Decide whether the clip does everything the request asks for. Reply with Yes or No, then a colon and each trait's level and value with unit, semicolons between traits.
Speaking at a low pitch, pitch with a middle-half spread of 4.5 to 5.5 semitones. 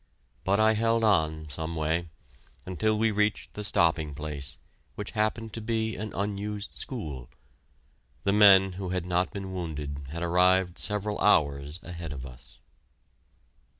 Yes: very low, 95 Hz; average, 5.0 semitones